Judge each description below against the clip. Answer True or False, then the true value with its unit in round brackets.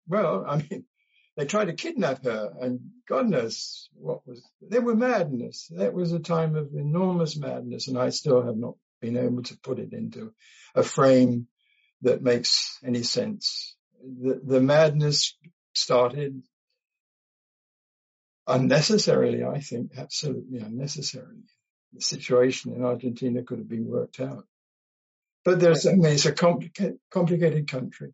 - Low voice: False (150 Hz)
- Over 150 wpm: False (145 wpm)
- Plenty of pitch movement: True (6.7 semitones)